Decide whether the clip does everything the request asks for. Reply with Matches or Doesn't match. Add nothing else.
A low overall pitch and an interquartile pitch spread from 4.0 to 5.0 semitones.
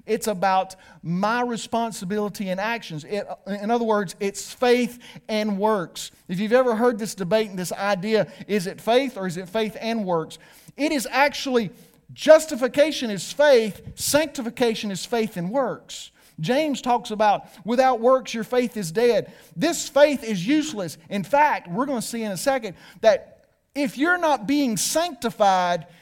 Doesn't match